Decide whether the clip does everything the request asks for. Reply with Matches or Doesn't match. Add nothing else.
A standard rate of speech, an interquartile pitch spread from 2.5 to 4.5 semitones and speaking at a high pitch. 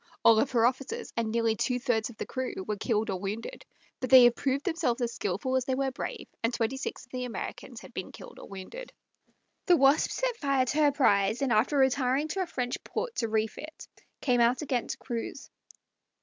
Doesn't match